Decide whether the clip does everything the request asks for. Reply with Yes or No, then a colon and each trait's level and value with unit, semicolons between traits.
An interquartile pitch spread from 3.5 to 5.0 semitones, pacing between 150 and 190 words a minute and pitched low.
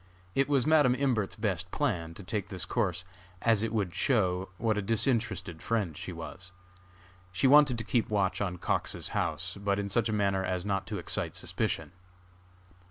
Yes: average, 3.9 semitones; average, 175 wpm; low, 100 Hz